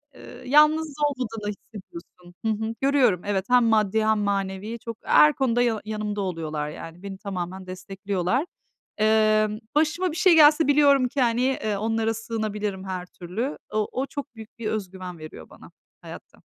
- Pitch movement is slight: No, average, 4.6 semitones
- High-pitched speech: Yes, high, 215 Hz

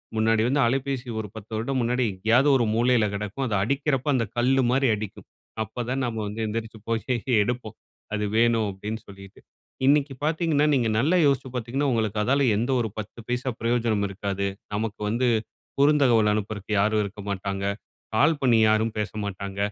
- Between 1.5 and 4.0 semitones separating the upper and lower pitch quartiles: Yes, average, 3.7 semitones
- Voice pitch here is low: Yes, low, 115 Hz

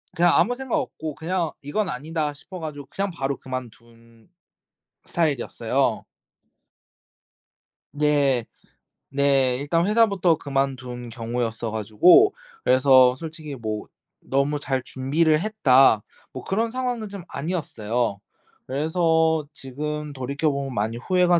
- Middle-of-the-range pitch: Yes, medium, 145 Hz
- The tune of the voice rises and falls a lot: No, average, 4.8 semitones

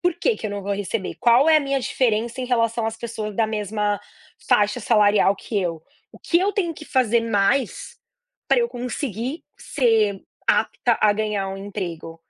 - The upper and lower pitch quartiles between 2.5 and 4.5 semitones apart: Yes, average, 3.6 semitones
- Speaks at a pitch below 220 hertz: No, high, 225 Hz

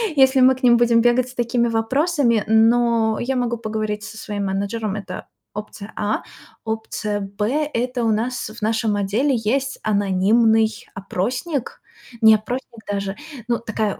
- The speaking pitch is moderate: No, high, 225 Hz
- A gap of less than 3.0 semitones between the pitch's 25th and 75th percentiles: Yes, narrow, 2.6 semitones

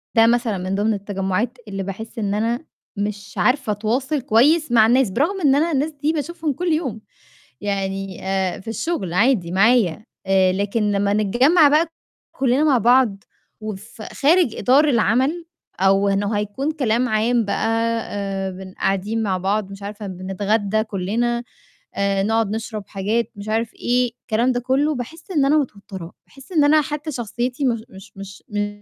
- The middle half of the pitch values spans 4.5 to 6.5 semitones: Yes, average, 4.9 semitones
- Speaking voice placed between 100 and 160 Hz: No, high, 220 Hz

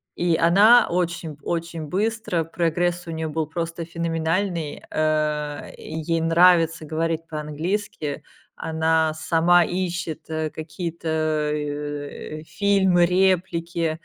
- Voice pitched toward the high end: No, medium, 165 Hz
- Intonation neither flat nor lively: No, narrow, 2.0 semitones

